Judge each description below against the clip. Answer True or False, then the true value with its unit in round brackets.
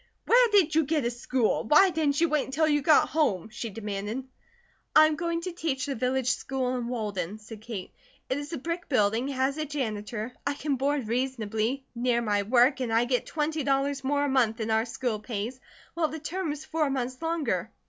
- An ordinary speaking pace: False (210 wpm)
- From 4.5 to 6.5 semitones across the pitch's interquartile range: True (4.8 semitones)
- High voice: True (265 Hz)